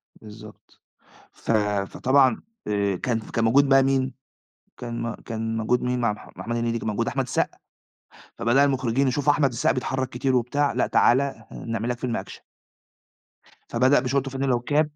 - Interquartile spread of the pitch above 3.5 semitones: No, average, 2.8 semitones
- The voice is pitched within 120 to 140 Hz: Yes, low, 125 Hz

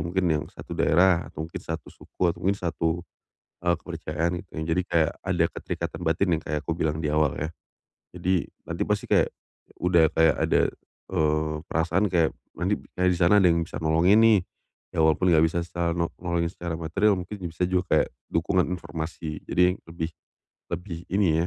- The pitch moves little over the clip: Yes, narrow, 2.0 semitones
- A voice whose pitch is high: No, very low, 85 Hz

